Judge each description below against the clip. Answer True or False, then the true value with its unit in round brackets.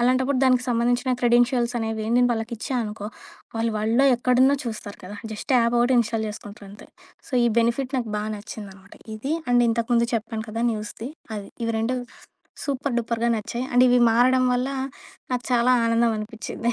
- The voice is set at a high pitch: True (235 Hz)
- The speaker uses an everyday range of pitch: False (2.0 semitones)